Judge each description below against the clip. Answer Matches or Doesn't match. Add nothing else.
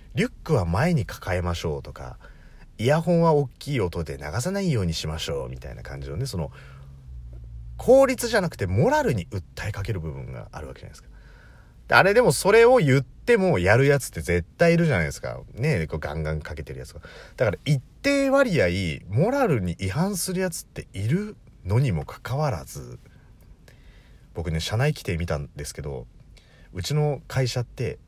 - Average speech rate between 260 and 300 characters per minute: Doesn't match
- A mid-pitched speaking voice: Doesn't match